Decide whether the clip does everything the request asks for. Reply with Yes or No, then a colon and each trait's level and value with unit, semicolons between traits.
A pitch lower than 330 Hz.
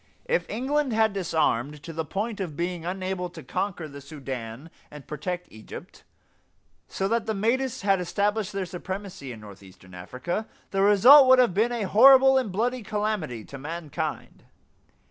Yes: high, 190 Hz